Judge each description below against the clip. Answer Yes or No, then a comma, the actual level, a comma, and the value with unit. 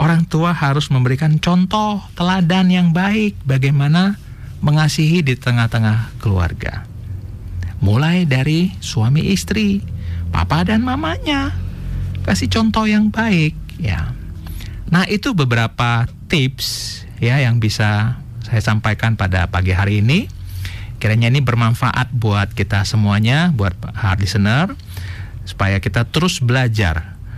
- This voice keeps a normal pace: Yes, average, 110 wpm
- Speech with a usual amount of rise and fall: No, wide, 7.5 semitones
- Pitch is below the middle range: Yes, low, 115 Hz